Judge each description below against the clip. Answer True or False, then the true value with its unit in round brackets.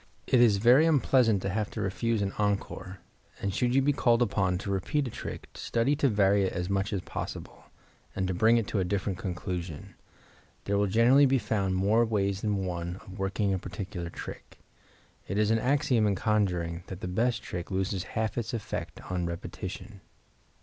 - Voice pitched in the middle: False (100 Hz)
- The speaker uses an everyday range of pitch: True (3.6 semitones)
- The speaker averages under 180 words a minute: False (190 wpm)